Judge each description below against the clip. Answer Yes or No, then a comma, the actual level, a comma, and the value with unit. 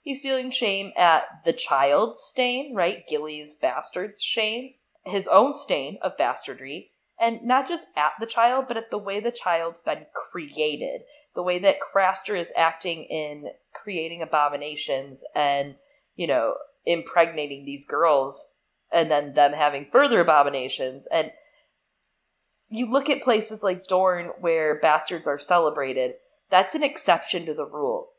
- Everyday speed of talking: Yes, average, 145 wpm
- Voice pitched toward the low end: No, high, 190 Hz